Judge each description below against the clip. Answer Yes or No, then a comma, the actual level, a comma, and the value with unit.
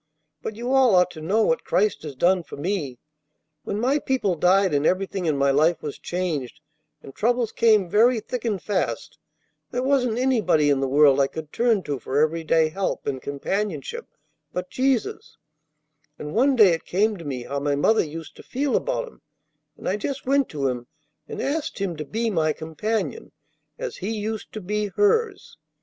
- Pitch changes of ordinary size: No, wide, 7.3 semitones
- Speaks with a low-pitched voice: No, high, 190 Hz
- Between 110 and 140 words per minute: No, average, 190 wpm